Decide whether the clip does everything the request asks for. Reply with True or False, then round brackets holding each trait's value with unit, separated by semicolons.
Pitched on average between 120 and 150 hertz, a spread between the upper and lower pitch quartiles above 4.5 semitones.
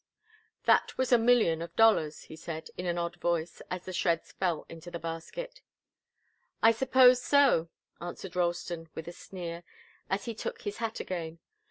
False (175 Hz; 5.2 semitones)